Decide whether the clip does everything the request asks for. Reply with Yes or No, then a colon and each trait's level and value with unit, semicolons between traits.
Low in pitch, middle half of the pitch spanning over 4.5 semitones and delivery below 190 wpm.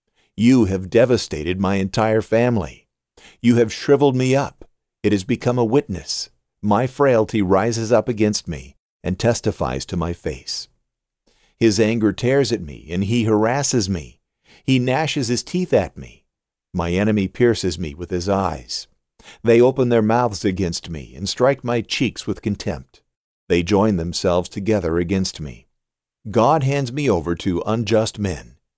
Yes: low, 105 Hz; average, 5.3 semitones; average, 155 wpm